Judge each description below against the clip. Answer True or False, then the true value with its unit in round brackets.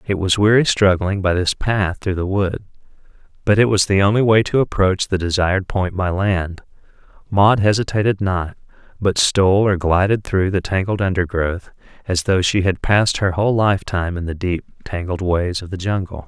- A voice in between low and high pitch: False (95 Hz)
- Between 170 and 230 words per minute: True (190 wpm)